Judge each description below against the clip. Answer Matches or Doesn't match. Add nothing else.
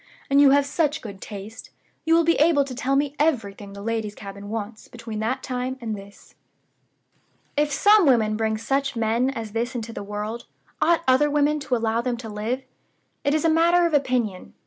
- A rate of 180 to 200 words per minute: Matches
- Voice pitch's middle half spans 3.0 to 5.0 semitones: Matches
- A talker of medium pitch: Doesn't match